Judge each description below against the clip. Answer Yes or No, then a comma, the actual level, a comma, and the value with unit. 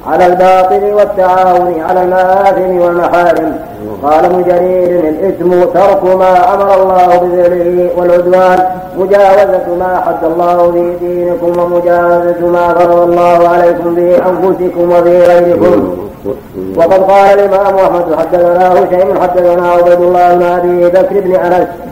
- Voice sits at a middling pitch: Yes, medium, 180 Hz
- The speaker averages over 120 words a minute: No, average, 110 wpm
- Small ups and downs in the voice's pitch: Yes, narrow, 1.1 semitones